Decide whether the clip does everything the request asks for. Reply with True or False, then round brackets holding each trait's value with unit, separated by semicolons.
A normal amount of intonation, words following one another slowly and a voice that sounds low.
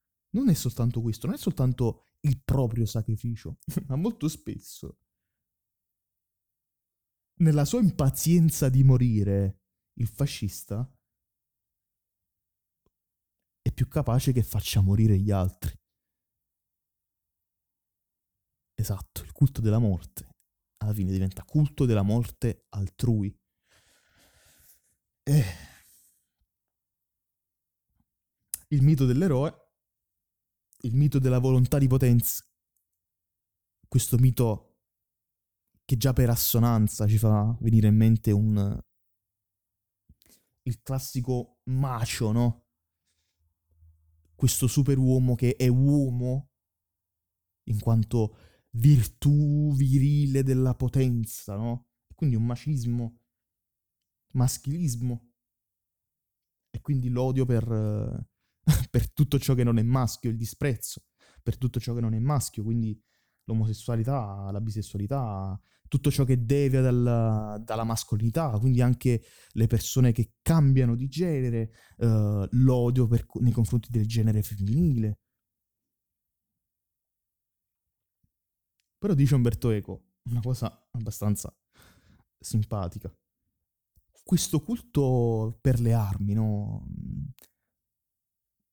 True (4.3 semitones; 95 wpm; 115 Hz)